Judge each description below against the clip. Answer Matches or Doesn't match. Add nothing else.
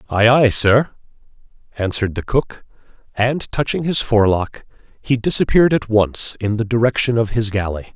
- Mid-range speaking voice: Doesn't match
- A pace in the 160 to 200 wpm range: Doesn't match